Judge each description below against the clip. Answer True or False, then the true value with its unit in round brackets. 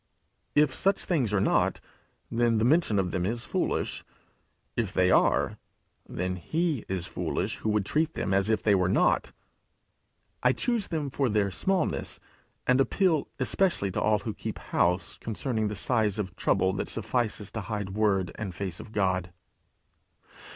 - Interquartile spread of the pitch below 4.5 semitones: False (5.2 semitones)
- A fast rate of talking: False (165 wpm)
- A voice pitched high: False (110 Hz)